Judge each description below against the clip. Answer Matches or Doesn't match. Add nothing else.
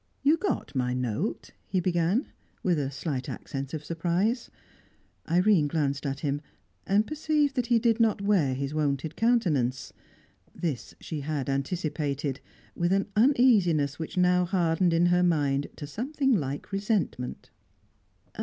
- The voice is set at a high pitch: Doesn't match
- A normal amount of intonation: Doesn't match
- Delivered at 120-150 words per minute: Matches